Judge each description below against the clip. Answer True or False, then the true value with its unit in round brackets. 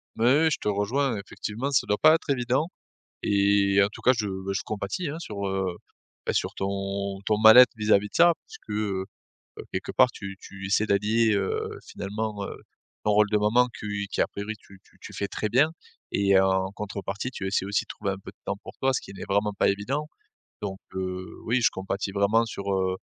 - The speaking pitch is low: True (100 Hz)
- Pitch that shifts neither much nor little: False (2.2 semitones)